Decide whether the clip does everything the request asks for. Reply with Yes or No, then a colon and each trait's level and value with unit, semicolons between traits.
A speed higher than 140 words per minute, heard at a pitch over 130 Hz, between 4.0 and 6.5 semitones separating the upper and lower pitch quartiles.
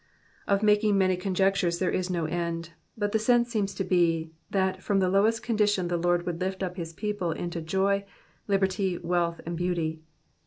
No: average, 185 wpm; medium, 185 Hz; narrow, 2.5 semitones